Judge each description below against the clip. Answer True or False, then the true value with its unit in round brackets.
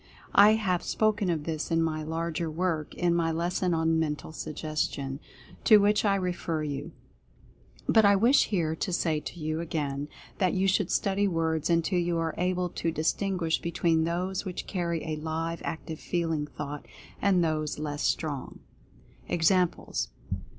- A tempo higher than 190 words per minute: False (155 wpm)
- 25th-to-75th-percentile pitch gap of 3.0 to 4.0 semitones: False (2.6 semitones)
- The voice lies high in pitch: False (165 Hz)